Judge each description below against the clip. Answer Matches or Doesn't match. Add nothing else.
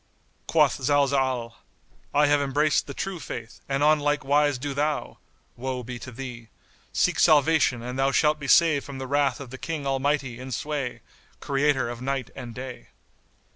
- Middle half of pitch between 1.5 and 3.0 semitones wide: Matches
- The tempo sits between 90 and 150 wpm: Doesn't match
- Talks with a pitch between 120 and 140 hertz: Matches